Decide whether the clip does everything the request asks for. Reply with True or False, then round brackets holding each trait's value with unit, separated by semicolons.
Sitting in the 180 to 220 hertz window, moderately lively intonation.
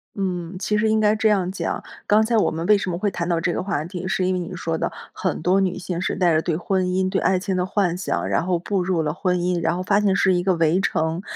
False (185 Hz; 1.9 semitones)